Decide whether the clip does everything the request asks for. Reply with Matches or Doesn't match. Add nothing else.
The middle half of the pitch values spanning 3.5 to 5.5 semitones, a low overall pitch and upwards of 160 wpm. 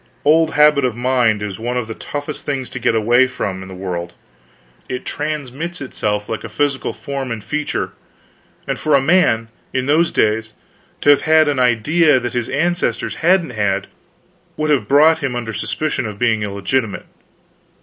Matches